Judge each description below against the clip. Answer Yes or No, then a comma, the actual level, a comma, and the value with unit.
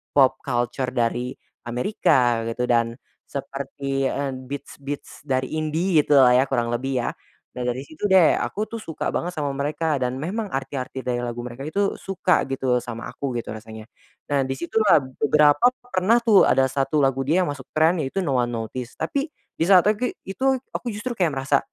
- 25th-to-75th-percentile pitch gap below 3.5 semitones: No, average, 5.0 semitones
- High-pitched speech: No, low, 135 Hz